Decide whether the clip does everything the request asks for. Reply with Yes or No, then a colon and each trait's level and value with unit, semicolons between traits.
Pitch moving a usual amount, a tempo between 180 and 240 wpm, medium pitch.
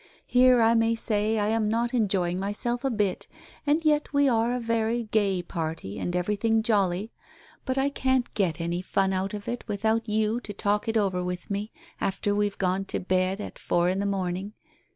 No: average, 3.3 semitones; average, 200 wpm; high, 210 Hz